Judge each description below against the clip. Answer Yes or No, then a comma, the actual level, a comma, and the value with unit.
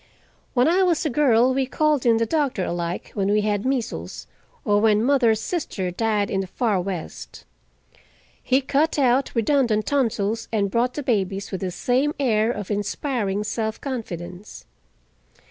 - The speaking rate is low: No, average, 160 wpm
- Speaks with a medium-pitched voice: No, high, 225 Hz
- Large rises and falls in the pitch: No, average, 4.7 semitones